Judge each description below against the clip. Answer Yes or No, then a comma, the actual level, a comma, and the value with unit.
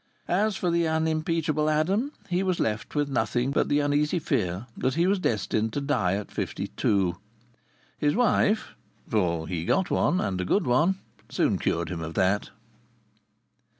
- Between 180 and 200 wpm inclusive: No, average, 165 wpm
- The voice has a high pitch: No, medium, 145 Hz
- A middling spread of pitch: No, wide, 9.0 semitones